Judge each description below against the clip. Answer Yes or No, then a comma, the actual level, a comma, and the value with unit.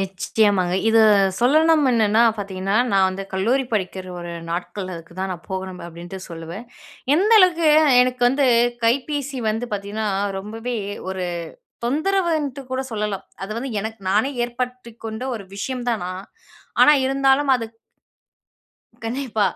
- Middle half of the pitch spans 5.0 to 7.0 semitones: Yes, wide, 5.5 semitones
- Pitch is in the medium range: No, high, 220 Hz